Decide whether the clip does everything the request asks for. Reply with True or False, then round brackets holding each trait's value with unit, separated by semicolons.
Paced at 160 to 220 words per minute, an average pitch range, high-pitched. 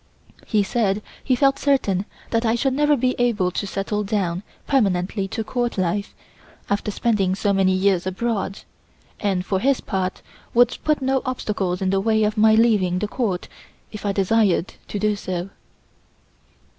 True (165 wpm; 3.7 semitones; 210 Hz)